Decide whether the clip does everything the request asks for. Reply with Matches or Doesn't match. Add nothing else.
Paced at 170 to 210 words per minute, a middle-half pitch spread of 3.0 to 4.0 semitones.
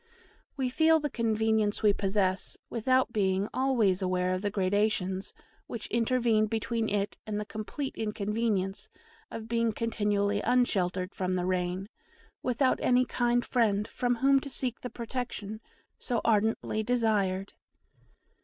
Doesn't match